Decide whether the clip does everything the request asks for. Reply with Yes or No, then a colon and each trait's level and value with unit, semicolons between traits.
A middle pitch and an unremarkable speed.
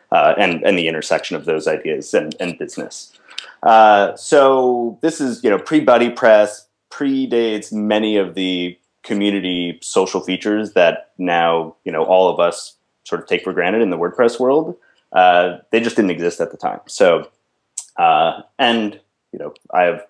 No: low, 105 Hz; average, 170 wpm